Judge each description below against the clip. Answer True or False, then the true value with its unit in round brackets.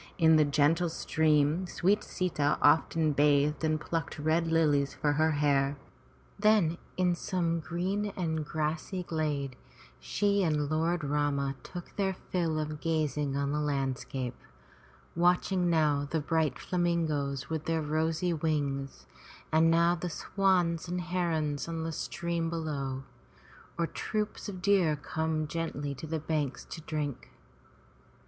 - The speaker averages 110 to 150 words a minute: True (140 wpm)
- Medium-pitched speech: True (160 Hz)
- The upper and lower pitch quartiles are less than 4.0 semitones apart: True (2.6 semitones)